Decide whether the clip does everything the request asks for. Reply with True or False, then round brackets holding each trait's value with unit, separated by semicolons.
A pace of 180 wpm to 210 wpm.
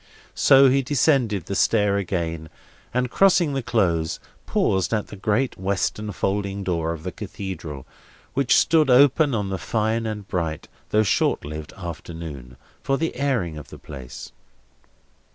False (150 wpm)